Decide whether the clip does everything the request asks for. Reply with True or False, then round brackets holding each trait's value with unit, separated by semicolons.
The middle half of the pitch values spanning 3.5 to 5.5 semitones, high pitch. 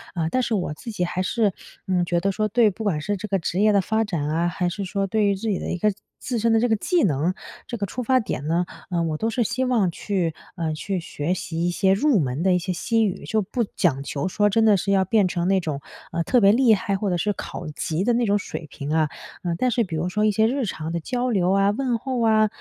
True (4.2 semitones; 195 Hz)